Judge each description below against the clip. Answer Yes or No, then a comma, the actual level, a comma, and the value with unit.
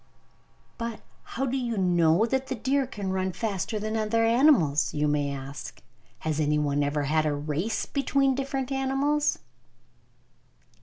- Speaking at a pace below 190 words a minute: Yes, average, 140 wpm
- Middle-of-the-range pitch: No, high, 215 Hz